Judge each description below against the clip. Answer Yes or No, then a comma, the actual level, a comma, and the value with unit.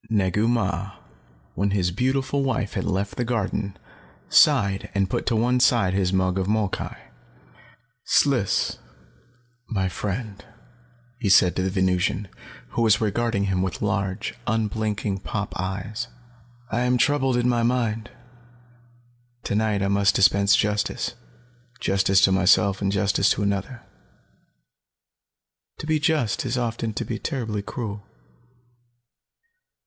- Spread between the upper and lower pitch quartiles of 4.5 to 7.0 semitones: No, average, 3.3 semitones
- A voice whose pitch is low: Yes, low, 105 Hz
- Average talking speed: No, slow, 130 wpm